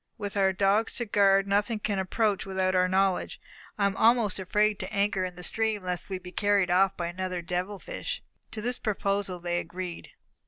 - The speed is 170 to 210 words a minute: Yes, average, 200 wpm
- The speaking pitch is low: No, high, 195 Hz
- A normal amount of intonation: No, narrow, 2.2 semitones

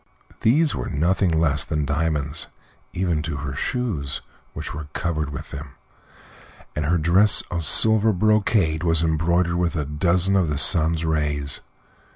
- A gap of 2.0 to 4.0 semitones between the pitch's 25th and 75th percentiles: Yes, average, 3.2 semitones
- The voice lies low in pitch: Yes, very low, 80 Hz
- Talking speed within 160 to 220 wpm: No, average, 150 wpm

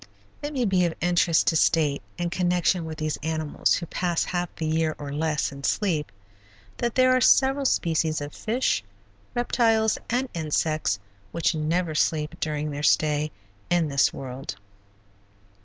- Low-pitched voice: No, medium, 160 Hz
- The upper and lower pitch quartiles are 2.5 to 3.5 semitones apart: Yes, average, 3.2 semitones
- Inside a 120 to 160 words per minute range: Yes, average, 155 wpm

